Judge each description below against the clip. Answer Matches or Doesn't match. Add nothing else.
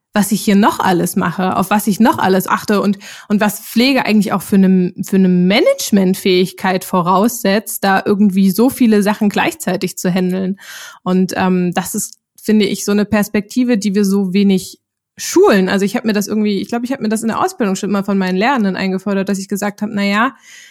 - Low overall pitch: Doesn't match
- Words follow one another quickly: Matches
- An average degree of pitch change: Doesn't match